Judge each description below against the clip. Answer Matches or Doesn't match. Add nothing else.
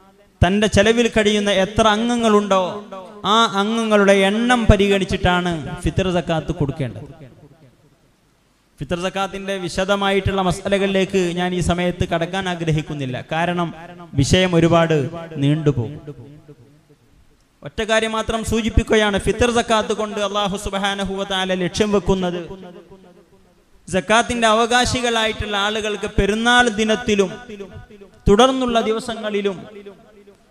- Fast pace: Doesn't match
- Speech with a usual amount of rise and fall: Matches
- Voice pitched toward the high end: Matches